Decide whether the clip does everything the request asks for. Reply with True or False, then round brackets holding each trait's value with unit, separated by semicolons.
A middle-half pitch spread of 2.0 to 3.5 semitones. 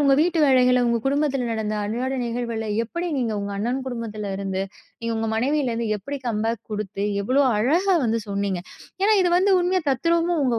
False (4.7 semitones)